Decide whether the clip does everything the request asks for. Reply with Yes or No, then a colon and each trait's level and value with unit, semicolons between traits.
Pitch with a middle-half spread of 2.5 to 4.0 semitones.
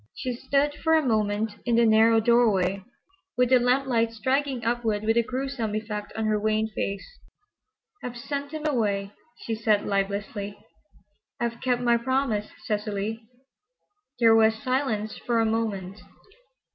Yes: average, 2.8 semitones